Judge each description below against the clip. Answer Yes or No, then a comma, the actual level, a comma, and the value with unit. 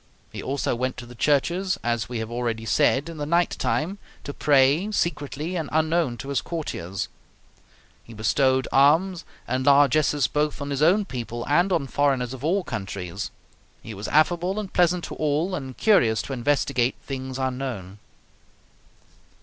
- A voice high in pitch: No, medium, 140 Hz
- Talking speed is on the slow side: No, average, 160 wpm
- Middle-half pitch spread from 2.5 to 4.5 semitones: No, average, 5.0 semitones